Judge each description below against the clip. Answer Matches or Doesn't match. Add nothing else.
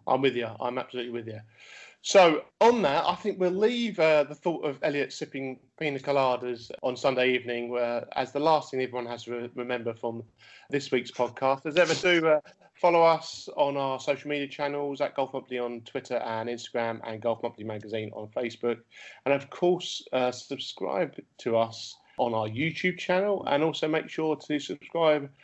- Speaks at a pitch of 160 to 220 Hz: Doesn't match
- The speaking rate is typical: Matches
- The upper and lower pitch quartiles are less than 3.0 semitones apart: Doesn't match